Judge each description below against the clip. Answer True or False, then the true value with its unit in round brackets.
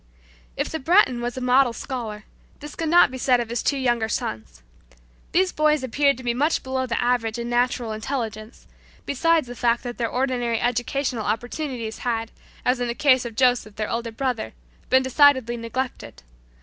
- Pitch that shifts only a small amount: True (2.3 semitones)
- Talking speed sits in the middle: True (180 wpm)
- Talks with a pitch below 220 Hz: False (245 Hz)